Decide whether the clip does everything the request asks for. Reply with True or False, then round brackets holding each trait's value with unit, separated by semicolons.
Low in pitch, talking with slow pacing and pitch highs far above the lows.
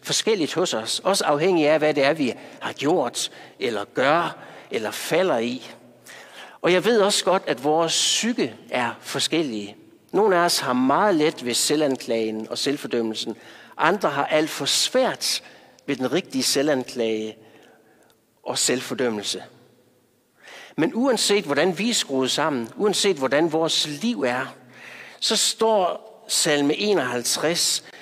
False (150 Hz; 135 wpm; 7.8 semitones)